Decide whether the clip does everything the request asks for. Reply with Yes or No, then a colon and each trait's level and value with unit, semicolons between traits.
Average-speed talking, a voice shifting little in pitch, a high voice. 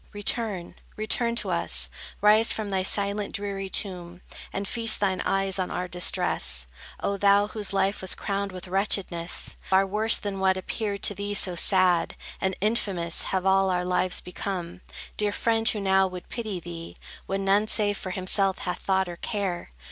Yes: average, 170 wpm; narrow, 1.9 semitones; high, 195 Hz